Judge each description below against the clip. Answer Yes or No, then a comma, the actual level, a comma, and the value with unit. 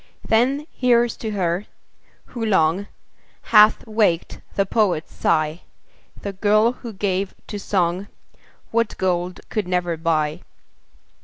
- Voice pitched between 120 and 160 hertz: No, high, 195 Hz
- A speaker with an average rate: No, slow, 120 wpm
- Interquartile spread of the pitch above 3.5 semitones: Yes, average, 4.0 semitones